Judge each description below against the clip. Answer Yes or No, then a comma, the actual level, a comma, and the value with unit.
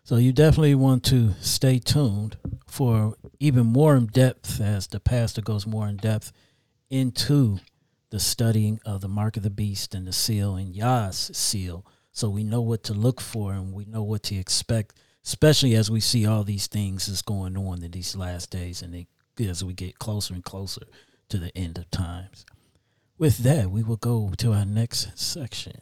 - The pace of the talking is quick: No, average, 195 wpm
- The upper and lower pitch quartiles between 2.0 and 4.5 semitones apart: Yes, average, 3.8 semitones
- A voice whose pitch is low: Yes, low, 110 Hz